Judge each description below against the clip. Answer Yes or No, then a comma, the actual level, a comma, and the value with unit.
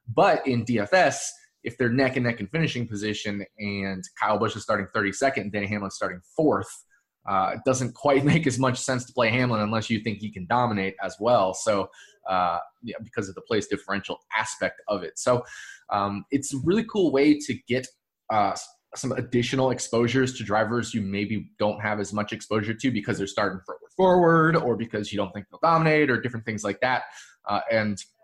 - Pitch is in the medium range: No, low, 120 Hz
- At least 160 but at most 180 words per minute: No, average, 195 wpm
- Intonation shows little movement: No, average, 4.3 semitones